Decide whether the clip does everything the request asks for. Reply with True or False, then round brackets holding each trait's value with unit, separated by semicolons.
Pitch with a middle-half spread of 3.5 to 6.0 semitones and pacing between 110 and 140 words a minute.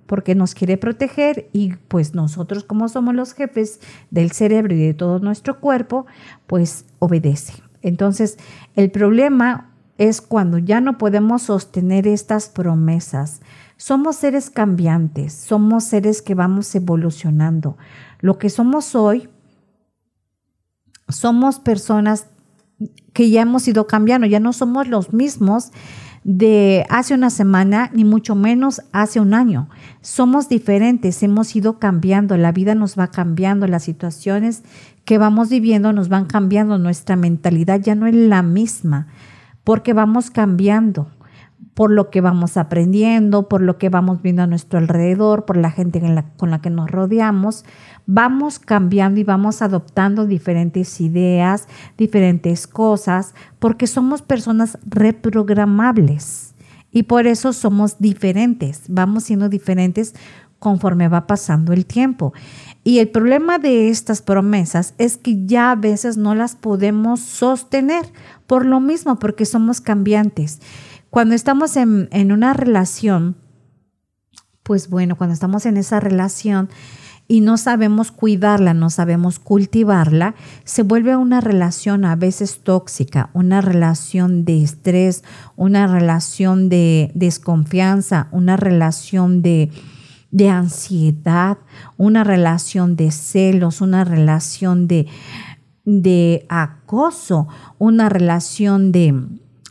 True (4.2 semitones; 130 wpm)